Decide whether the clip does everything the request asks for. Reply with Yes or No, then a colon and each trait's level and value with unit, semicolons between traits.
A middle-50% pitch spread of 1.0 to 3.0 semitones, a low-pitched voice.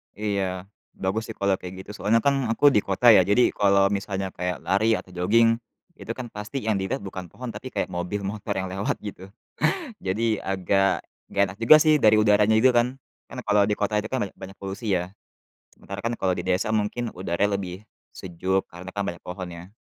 Yes: average, 2.7 semitones; low, 100 Hz